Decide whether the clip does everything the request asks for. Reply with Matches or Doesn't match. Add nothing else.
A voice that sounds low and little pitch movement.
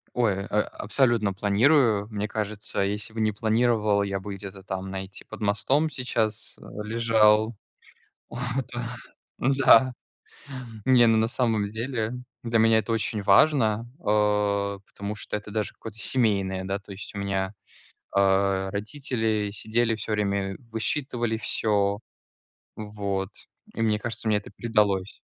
Matches